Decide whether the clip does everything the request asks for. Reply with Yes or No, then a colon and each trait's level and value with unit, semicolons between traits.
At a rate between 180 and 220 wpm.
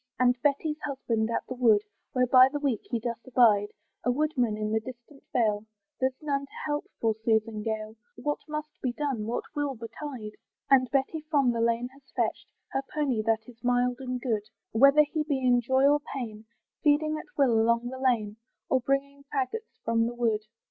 Yes: average, 190 wpm